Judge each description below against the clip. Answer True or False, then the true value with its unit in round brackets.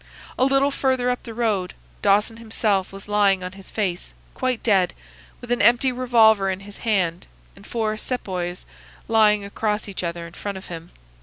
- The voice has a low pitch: False (210 Hz)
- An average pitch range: True (3.7 semitones)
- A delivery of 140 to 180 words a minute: True (175 wpm)